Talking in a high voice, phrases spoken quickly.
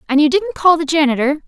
Yes: very high, 310 Hz; fast, 245 wpm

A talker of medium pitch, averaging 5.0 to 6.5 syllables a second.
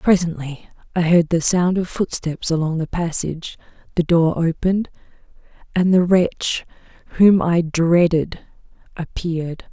No: medium, 170 Hz; 4.5 syllables/s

